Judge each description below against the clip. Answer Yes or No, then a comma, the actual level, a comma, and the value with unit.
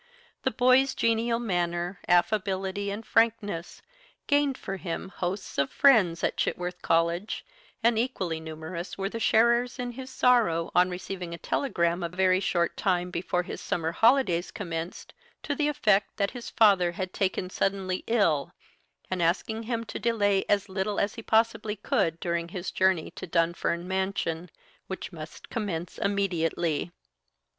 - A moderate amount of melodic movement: Yes, average, 4.4 semitones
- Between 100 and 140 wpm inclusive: No, average, 150 wpm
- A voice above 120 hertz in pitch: Yes, high, 190 Hz